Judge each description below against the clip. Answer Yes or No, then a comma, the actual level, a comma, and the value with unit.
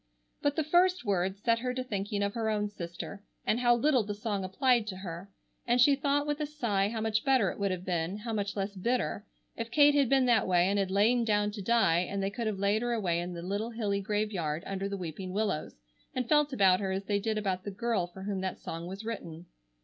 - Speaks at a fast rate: Yes, fast, 245 wpm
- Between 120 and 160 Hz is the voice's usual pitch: No, high, 205 Hz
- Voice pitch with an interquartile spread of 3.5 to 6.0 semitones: Yes, average, 3.8 semitones